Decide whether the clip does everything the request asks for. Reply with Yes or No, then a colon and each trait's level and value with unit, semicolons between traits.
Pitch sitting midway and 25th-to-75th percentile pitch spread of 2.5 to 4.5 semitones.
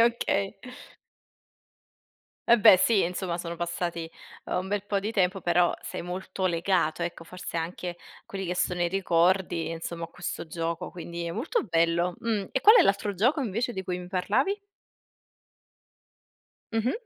Yes: medium, 180 Hz; average, 2.8 semitones